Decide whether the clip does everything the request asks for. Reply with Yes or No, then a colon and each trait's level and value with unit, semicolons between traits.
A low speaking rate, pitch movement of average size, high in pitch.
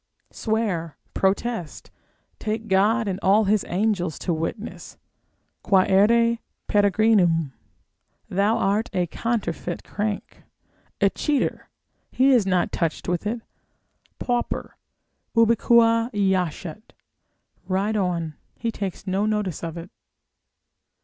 Yes: slow, 105 wpm; average, 3.8 semitones; high, 200 Hz